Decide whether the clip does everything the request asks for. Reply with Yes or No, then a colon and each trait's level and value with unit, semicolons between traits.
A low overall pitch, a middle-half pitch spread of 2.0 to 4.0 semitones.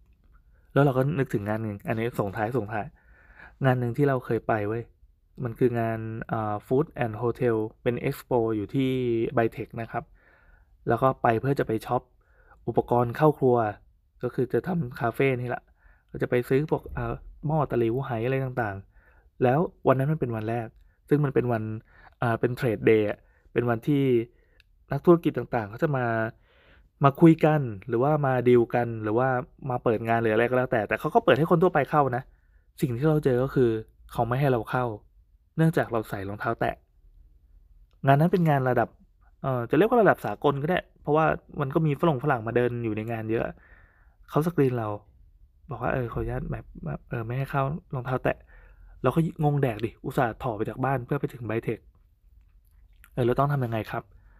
Yes: low, 120 Hz; average, 3.7 semitones